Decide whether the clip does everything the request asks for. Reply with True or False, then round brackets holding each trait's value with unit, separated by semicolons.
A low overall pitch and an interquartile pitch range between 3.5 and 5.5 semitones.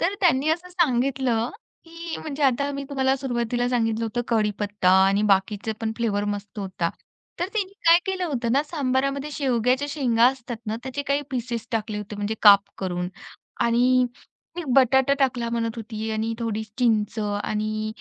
False (240 Hz; 4.2 semitones)